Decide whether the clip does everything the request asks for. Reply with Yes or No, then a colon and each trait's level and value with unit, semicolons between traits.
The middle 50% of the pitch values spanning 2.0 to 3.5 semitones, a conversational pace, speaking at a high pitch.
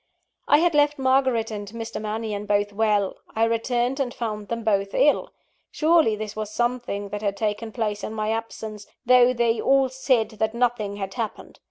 Yes: average, 2.8 semitones; average, 180 wpm; high, 225 Hz